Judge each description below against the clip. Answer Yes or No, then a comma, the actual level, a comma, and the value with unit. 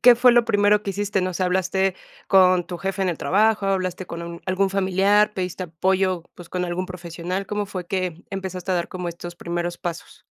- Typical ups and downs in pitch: No, narrow, 1.9 semitones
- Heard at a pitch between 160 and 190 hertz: Yes, medium, 185 Hz